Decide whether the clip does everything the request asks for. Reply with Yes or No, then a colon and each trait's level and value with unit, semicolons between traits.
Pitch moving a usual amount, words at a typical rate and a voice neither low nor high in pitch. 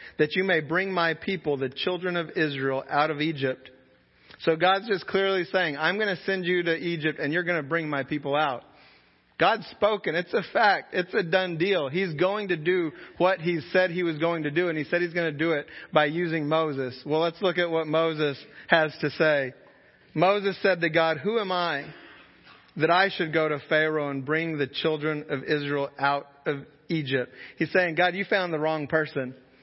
No: average, 3.2 semitones; fast, 210 wpm; medium, 160 Hz